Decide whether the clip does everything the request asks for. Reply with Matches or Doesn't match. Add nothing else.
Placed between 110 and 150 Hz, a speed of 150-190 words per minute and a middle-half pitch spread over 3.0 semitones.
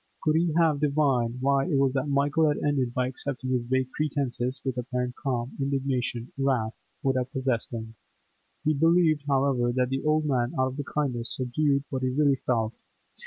Doesn't match